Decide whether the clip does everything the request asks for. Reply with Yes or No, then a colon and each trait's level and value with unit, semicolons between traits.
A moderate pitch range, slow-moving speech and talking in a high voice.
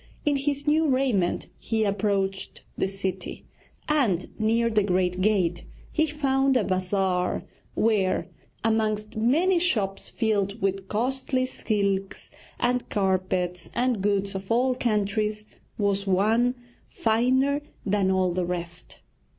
Yes: average, 4.5 semitones; slow, 120 wpm; high, 210 Hz